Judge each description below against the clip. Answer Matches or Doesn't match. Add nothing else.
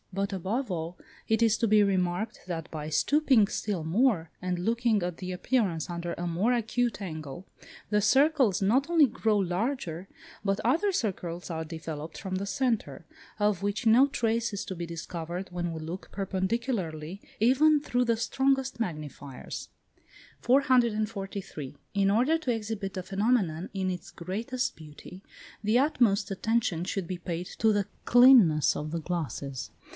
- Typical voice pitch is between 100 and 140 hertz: Doesn't match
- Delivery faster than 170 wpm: Doesn't match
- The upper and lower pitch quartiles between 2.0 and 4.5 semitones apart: Doesn't match